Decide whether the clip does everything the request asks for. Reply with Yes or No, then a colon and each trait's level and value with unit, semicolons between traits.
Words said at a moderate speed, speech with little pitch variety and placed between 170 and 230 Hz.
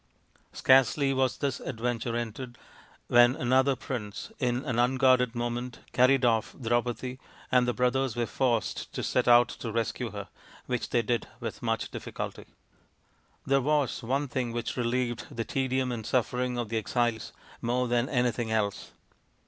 No: average, 155 wpm; narrow, 1.6 semitones; low, 125 Hz